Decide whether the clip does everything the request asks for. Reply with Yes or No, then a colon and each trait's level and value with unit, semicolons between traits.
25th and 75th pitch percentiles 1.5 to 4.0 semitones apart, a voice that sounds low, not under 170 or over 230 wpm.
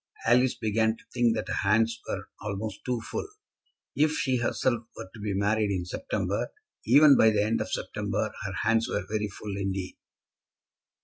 Yes: average, 2.7 semitones; low, 110 Hz; average, 175 wpm